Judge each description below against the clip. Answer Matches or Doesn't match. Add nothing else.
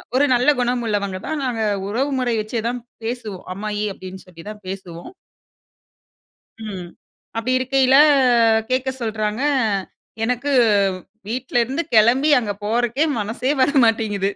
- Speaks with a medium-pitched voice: Doesn't match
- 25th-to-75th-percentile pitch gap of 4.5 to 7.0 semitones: Doesn't match